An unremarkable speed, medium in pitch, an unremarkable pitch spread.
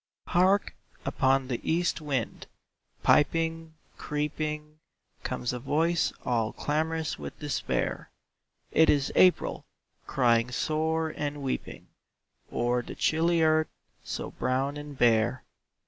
No: slow, 110 wpm; medium, 150 Hz; average, 3.7 semitones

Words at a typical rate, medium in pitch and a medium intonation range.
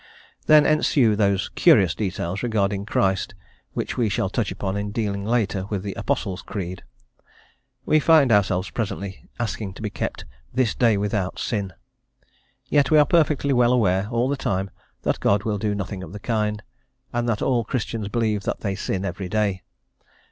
No: average, 170 wpm; low, 105 Hz; average, 3.4 semitones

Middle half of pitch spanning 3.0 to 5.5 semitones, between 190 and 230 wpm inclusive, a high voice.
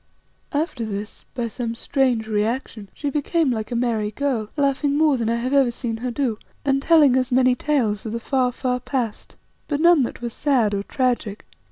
Yes: average, 3.7 semitones; average, 195 wpm; very high, 250 Hz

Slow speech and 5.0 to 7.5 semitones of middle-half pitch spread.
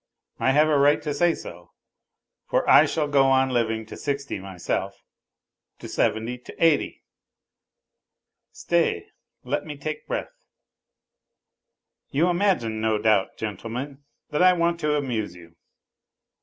Yes: slow, 130 wpm; average, 5.3 semitones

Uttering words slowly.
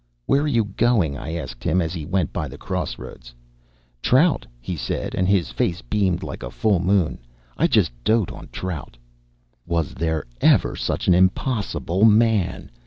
No: average, 175 wpm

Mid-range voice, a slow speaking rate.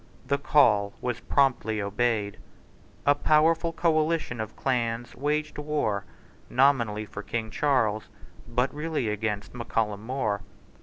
No: low, 120 Hz; slow, 120 wpm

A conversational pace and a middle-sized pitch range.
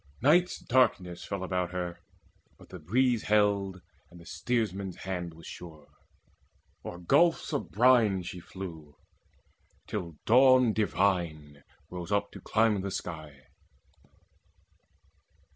No: slow, 115 wpm; average, 4.2 semitones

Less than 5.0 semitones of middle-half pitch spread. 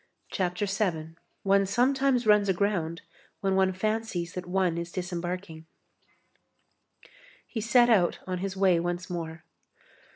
Yes: average, 2.8 semitones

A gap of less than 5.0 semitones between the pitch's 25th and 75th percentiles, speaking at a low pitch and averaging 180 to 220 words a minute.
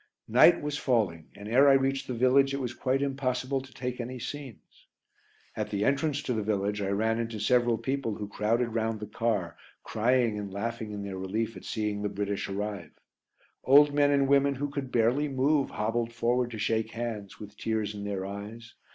Yes: average, 4.2 semitones; low, 115 Hz; average, 195 wpm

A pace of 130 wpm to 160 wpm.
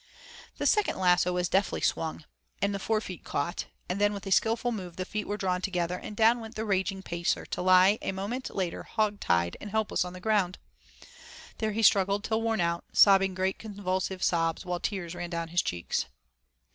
No: average, 195 wpm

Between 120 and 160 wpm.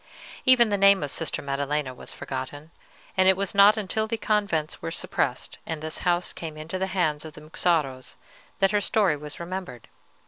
No: average, 185 wpm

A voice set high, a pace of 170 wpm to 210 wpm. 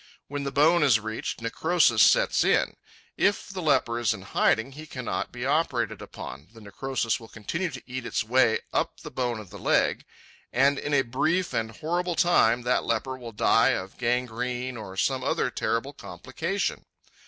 No: low, 125 Hz; average, 175 wpm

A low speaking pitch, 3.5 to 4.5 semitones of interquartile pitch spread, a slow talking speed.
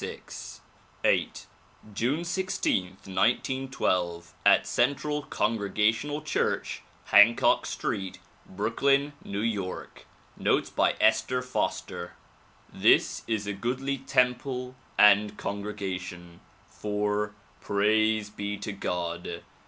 Yes: low, 105 Hz; average, 4.2 semitones; slow, 90 wpm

